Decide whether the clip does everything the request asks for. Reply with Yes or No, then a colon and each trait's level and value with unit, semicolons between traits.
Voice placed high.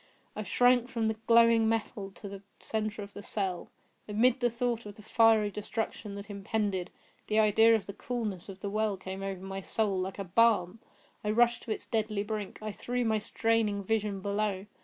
Yes: high, 215 Hz